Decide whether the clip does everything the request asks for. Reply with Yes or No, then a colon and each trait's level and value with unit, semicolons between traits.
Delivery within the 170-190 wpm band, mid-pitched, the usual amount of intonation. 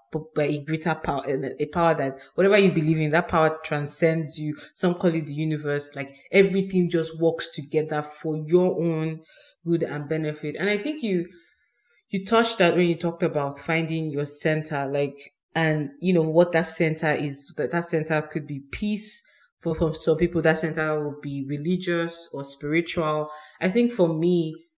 No: average, 180 wpm; medium, 160 Hz; narrow, 2.3 semitones